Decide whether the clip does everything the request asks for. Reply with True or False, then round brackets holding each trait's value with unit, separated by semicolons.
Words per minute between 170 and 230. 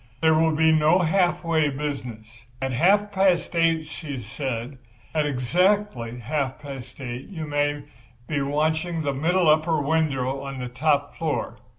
False (155 wpm)